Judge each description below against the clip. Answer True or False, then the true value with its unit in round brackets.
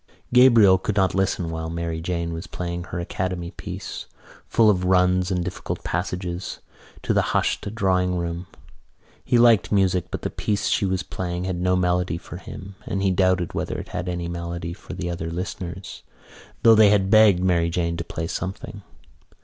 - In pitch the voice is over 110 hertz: False (90 Hz)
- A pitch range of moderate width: False (1.9 semitones)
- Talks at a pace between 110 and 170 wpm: False (180 wpm)